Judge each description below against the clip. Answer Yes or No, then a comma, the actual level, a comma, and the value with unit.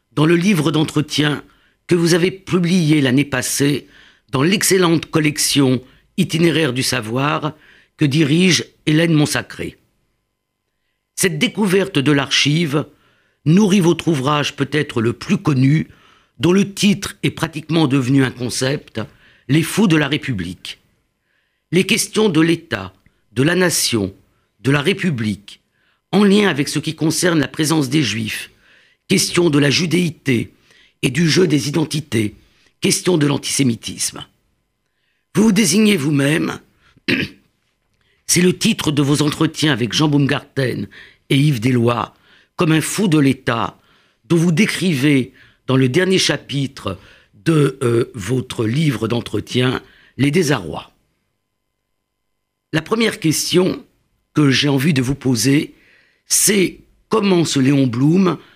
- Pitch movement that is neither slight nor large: Yes, average, 4.6 semitones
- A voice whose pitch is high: No, medium, 150 Hz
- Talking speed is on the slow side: Yes, slow, 130 wpm